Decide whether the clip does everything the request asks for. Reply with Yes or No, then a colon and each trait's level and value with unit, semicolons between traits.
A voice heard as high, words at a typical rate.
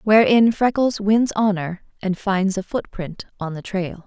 Yes: high, 200 Hz; average, 160 wpm